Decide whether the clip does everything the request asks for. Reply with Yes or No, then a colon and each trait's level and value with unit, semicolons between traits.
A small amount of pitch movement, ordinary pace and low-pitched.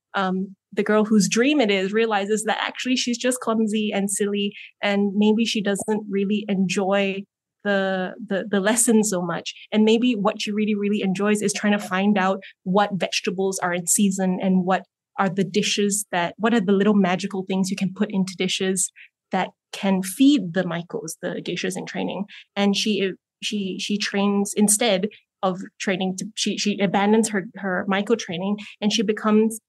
No: narrow, 1.8 semitones; average, 180 wpm; high, 200 Hz